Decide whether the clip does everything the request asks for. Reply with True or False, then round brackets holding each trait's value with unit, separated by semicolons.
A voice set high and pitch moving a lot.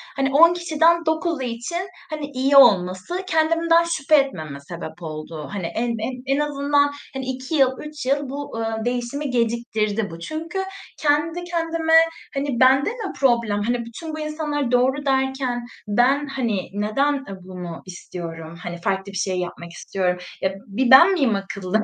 True (260 Hz; 6.5 semitones)